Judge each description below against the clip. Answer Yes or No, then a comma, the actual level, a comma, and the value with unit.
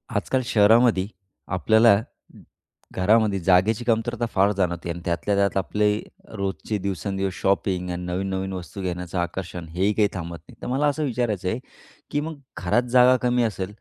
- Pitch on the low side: Yes, low, 100 Hz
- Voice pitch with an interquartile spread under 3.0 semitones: No, average, 3.6 semitones